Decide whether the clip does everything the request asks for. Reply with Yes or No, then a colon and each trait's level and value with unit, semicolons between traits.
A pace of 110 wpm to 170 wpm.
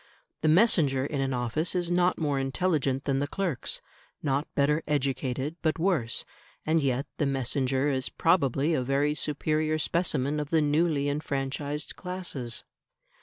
Yes: average, 145 wpm